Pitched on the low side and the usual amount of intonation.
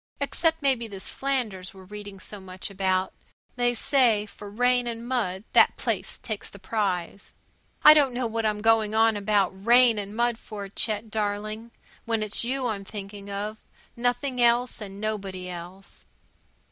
No: high, 215 Hz; average, 3.2 semitones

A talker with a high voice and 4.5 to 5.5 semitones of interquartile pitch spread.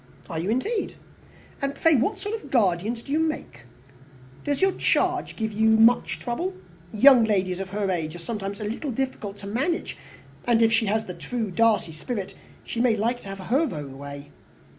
Yes: high, 220 Hz; average, 5.2 semitones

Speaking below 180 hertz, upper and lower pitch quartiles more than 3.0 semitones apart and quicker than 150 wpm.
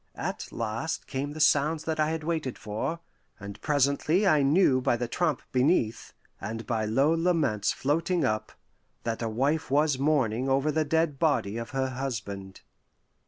Yes: medium, 140 Hz; average, 5.2 semitones; average, 165 wpm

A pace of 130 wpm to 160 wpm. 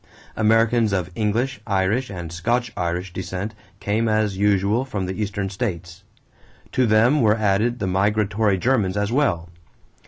Yes: average, 145 wpm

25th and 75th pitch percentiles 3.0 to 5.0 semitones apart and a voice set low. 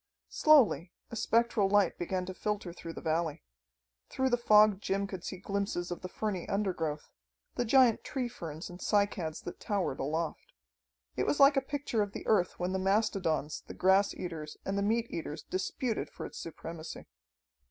No: average, 4.1 semitones; high, 195 Hz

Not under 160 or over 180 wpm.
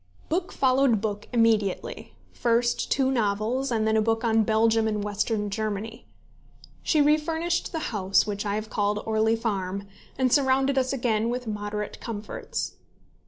No: average, 150 wpm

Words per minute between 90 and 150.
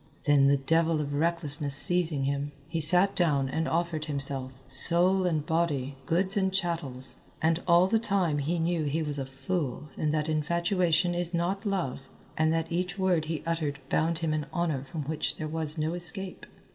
No: average, 185 wpm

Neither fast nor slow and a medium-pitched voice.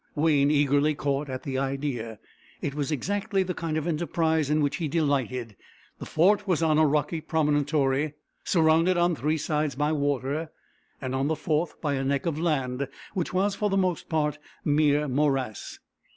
Yes: average, 175 wpm; medium, 150 Hz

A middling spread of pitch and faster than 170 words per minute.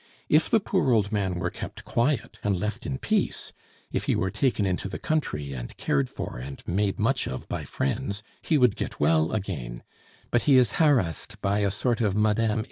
No: wide, 5.9 semitones; average, 200 wpm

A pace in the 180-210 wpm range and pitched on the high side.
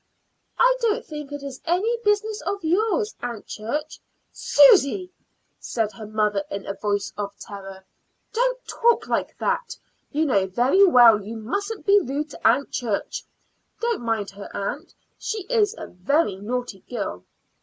No: average, 155 wpm; very high, 275 Hz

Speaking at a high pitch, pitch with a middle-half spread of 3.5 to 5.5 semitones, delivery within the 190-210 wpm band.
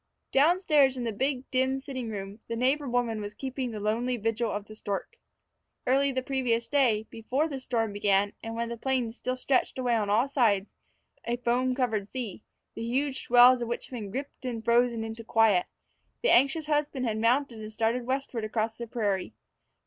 No: high, 240 Hz; average, 2.9 semitones; average, 195 wpm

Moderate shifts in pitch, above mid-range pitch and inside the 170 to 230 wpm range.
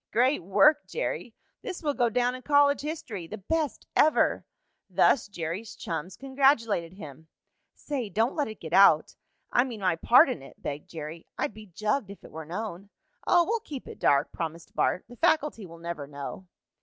No: wide, 8.4 semitones; high, 215 Hz; average, 180 wpm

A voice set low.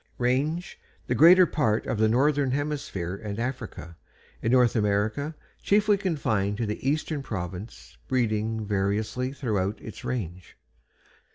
Yes: low, 115 Hz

